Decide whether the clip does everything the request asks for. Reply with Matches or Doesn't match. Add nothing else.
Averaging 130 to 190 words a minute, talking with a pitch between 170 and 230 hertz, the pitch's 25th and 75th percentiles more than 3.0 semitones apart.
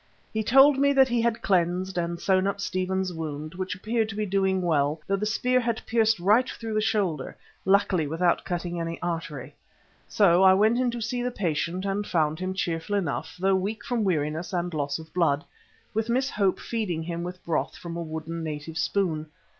Doesn't match